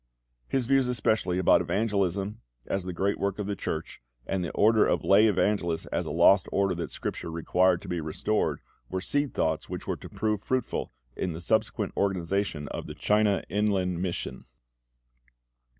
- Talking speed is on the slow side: No, average, 170 wpm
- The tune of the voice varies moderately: Yes, average, 3.1 semitones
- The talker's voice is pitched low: Yes, low, 100 Hz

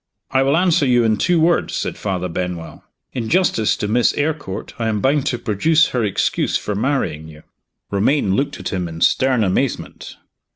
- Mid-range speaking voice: No, low, 115 Hz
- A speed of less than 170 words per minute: No, average, 180 wpm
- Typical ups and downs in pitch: No, wide, 6.6 semitones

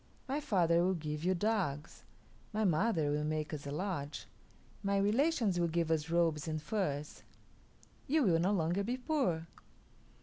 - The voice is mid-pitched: Yes, medium, 170 Hz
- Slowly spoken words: No, average, 160 wpm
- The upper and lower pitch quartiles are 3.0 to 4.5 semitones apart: No, average, 5.0 semitones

